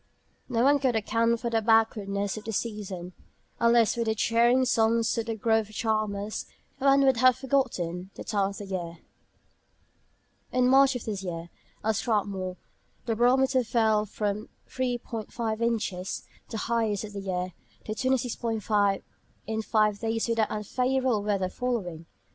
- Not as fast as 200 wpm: Yes, average, 145 wpm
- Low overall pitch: No, high, 220 Hz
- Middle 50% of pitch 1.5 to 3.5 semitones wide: Yes, average, 2.7 semitones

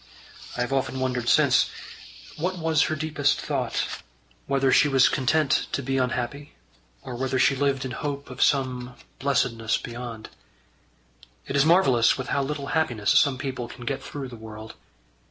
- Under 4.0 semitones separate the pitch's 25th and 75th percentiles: Yes, narrow, 2.4 semitones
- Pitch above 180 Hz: No, low, 135 Hz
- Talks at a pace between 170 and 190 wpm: No, average, 160 wpm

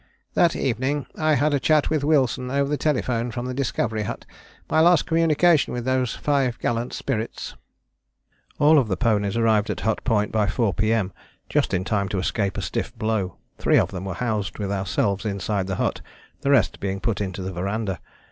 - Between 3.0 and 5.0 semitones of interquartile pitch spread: No, wide, 5.5 semitones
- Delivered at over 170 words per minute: Yes, average, 190 wpm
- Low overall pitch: Yes, low, 115 Hz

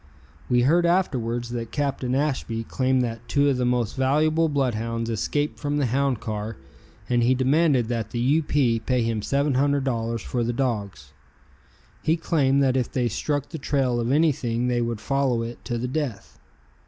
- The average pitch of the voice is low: Yes, low, 125 Hz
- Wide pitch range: No, average, 3.4 semitones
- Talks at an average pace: Yes, average, 180 wpm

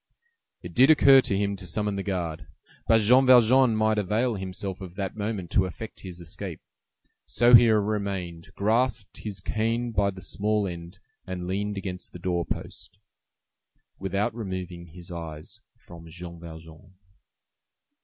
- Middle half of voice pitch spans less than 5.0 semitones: Yes, average, 3.5 semitones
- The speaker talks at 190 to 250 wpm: No, average, 150 wpm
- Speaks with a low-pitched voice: Yes, low, 100 Hz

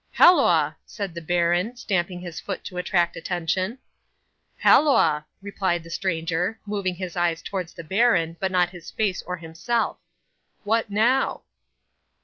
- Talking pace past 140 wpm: No, slow, 135 wpm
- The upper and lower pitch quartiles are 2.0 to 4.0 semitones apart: Yes, average, 3.1 semitones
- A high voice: No, medium, 180 Hz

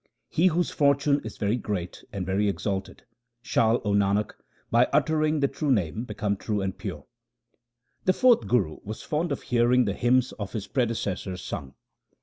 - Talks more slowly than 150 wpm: No, average, 165 wpm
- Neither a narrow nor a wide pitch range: No, wide, 5.8 semitones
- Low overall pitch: Yes, low, 115 Hz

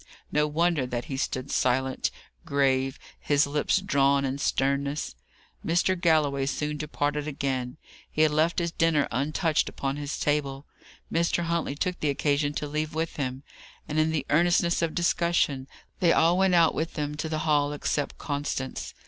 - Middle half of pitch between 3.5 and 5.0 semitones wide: No, average, 2.8 semitones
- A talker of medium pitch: Yes, medium, 150 Hz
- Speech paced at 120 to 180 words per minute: Yes, average, 165 wpm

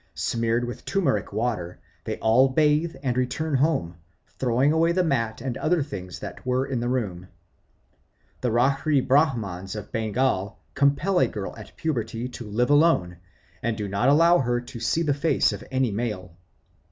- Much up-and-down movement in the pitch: No, average, 4.8 semitones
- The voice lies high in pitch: No, low, 125 Hz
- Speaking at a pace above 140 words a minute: Yes, average, 165 wpm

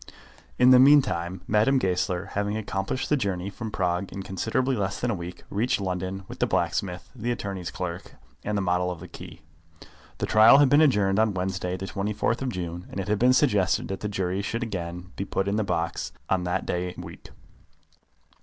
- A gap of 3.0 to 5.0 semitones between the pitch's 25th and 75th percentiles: Yes, average, 3.5 semitones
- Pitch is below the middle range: Yes, low, 100 Hz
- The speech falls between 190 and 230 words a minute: Yes, average, 200 wpm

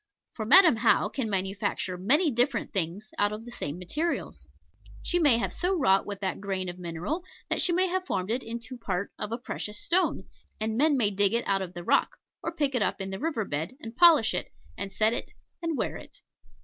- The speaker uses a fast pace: Yes, fast, 220 wpm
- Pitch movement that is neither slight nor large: No, wide, 6.9 semitones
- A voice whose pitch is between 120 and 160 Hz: No, high, 220 Hz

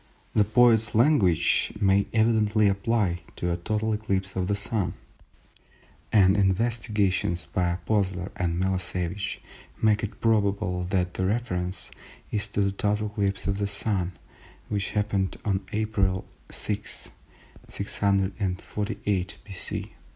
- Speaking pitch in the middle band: No, low, 100 Hz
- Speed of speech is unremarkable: No, slow, 120 wpm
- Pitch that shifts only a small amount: Yes, narrow, 2.3 semitones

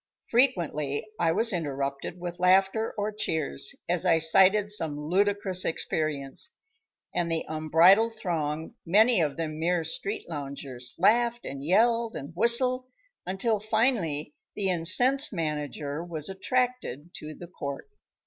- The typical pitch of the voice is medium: Yes, medium, 175 Hz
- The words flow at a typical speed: No, slow, 130 wpm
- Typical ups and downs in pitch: No, wide, 5.8 semitones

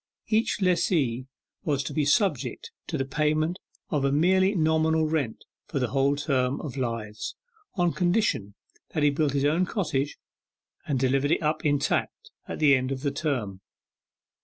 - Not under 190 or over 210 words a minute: No, average, 160 wpm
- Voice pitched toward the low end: No, medium, 145 Hz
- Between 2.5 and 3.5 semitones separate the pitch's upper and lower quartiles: Yes, average, 3.1 semitones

